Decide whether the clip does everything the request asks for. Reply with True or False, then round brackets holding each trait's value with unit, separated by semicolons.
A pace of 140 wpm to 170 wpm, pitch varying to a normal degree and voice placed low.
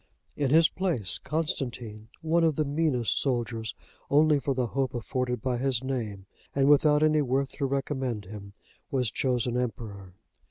True (155 wpm; 3.9 semitones; 130 Hz)